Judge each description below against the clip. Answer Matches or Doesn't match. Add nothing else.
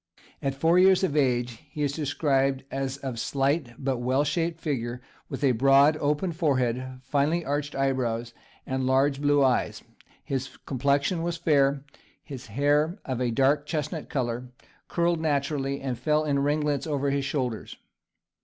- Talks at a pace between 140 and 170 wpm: Matches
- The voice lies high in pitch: Doesn't match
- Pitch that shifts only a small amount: Matches